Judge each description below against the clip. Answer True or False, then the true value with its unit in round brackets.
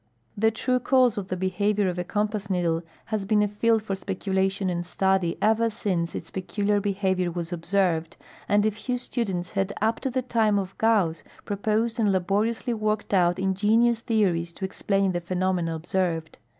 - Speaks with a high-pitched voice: True (195 Hz)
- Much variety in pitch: False (3.0 semitones)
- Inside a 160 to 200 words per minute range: True (175 wpm)